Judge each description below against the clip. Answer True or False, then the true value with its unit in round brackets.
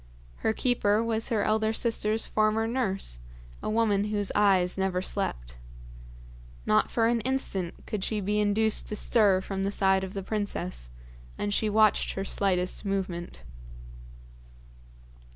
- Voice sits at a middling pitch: False (205 Hz)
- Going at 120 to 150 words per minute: True (140 wpm)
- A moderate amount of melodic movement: False (2.3 semitones)